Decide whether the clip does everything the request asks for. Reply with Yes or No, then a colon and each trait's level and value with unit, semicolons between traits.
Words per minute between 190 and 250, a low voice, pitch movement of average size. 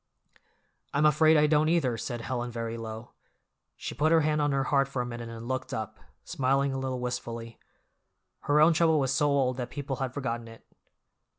Yes: average, 195 wpm; low, 130 Hz; average, 3.8 semitones